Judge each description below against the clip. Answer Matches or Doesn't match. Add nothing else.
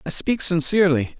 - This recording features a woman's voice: Doesn't match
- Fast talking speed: Doesn't match